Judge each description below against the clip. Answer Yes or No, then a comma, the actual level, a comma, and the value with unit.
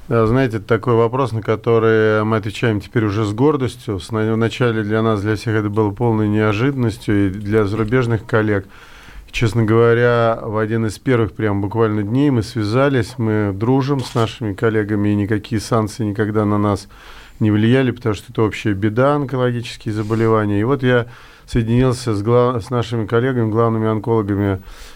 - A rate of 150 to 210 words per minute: Yes, fast, 160 wpm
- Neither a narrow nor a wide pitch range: No, narrow, 1.9 semitones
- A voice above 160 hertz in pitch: No, low, 110 Hz